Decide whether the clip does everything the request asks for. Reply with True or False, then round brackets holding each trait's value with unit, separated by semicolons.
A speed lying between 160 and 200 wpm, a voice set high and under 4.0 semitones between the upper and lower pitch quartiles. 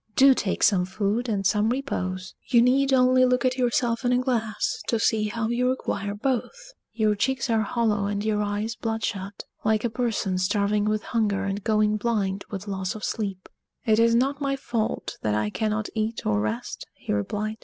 True (190 wpm; 220 Hz; 3.0 semitones)